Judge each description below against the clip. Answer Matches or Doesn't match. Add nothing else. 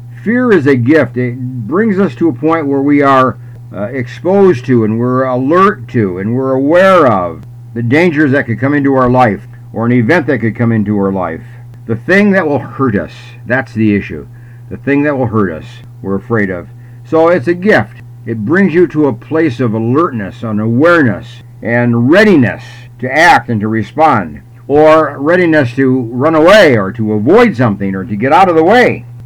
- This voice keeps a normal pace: Matches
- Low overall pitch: Matches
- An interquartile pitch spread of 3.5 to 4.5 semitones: Matches